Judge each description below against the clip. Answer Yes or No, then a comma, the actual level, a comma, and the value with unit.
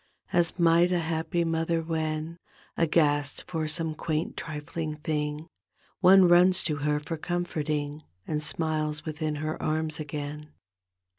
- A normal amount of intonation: No, narrow, 1.8 semitones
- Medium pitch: Yes, medium, 155 Hz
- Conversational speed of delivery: No, slow, 130 wpm